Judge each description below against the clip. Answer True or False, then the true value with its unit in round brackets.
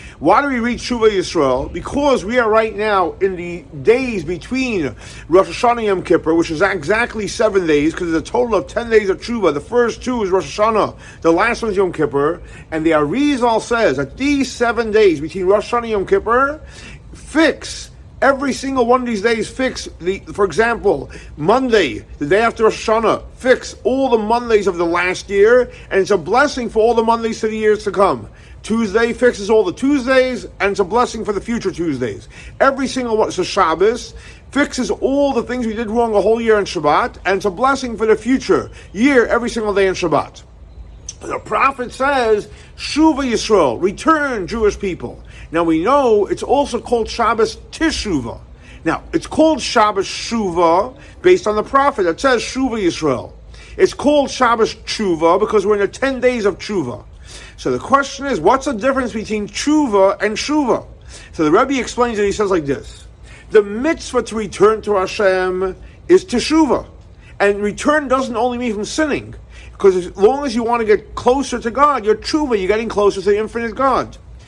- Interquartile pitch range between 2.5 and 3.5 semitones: False (4.7 semitones)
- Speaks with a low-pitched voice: False (230 Hz)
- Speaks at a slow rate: False (190 wpm)